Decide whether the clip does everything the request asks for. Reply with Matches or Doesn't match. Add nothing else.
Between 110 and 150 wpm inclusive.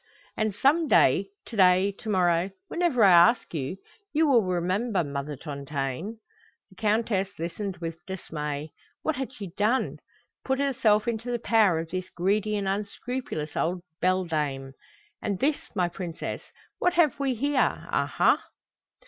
Matches